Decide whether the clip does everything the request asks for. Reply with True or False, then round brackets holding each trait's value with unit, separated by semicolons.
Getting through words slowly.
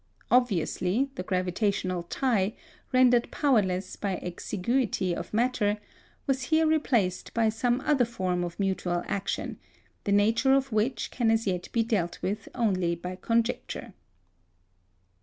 True (130 wpm)